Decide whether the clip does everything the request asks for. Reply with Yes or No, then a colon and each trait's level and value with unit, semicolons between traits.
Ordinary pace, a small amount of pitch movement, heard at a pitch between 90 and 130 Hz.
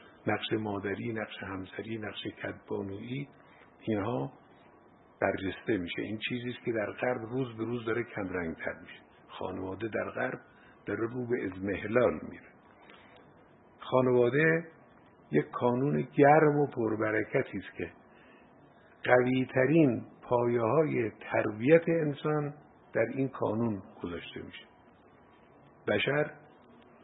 No: average, 115 wpm; average, 3.8 semitones; low, 120 Hz